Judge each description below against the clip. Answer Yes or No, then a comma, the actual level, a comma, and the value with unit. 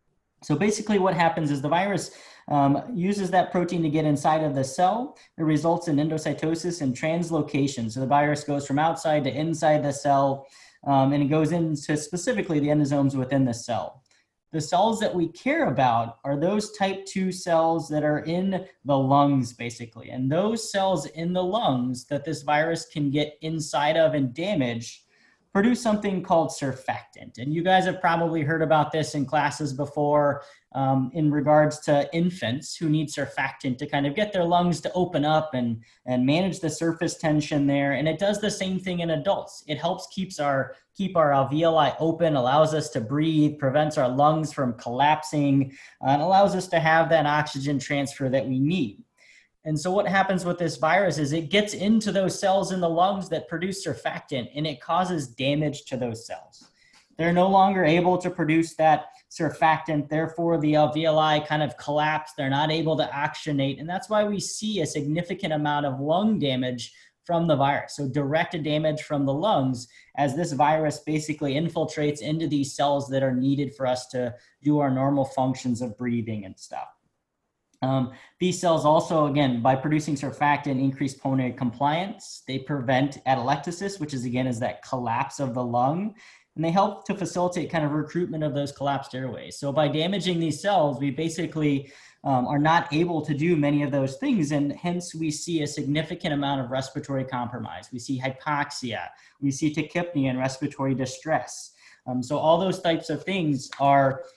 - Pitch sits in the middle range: Yes, medium, 150 Hz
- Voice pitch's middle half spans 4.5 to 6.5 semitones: No, average, 3.3 semitones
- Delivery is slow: No, average, 180 wpm